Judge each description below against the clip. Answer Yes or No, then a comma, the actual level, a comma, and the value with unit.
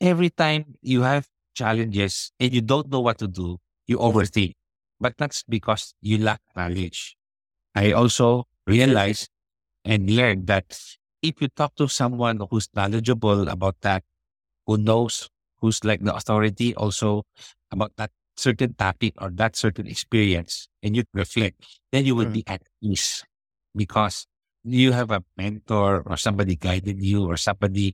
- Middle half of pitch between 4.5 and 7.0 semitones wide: No, average, 3.6 semitones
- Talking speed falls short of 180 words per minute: Yes, average, 150 wpm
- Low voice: Yes, low, 110 Hz